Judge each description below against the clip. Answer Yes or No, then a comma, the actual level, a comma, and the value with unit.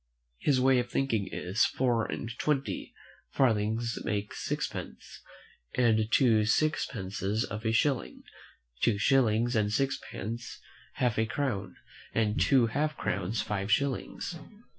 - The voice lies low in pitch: Yes, low, 115 Hz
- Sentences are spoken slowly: Yes, slow, 120 wpm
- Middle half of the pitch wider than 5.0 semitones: No, average, 3.7 semitones